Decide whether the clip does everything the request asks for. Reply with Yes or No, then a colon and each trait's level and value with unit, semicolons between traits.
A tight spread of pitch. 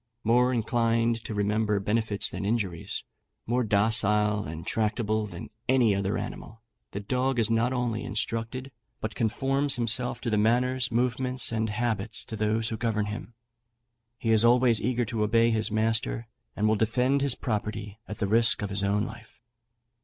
Yes: narrow, 2.3 semitones